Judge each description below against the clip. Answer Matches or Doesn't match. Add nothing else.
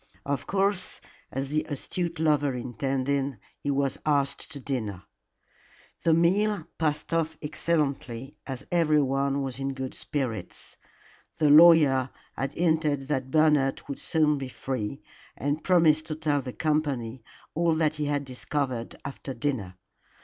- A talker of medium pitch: Matches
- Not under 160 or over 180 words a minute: Doesn't match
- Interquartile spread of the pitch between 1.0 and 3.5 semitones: Matches